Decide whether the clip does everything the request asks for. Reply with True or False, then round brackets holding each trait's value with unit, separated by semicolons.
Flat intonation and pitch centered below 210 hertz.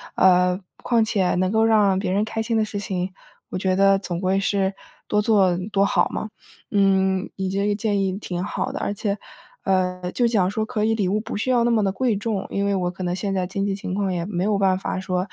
True (2.1 semitones; 195 Hz)